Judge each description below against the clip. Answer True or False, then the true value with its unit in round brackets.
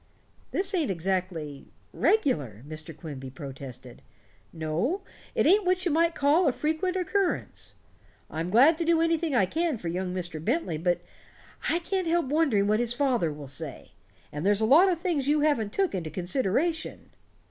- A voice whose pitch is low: False (240 Hz)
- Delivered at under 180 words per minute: True (170 wpm)